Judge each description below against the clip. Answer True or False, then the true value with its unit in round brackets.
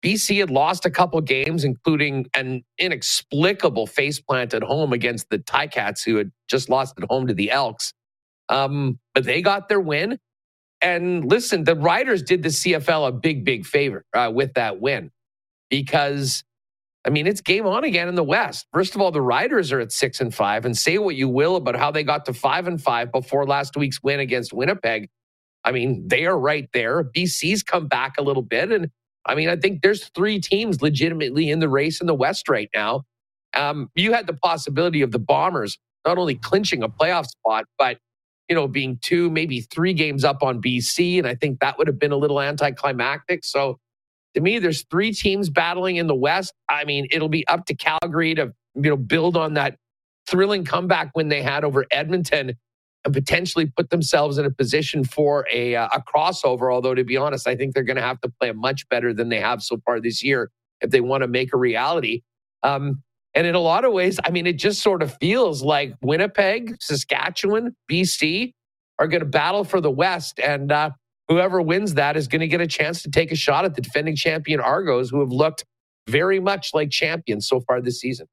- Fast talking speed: True (210 wpm)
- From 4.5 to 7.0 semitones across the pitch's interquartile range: True (4.9 semitones)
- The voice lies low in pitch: False (145 Hz)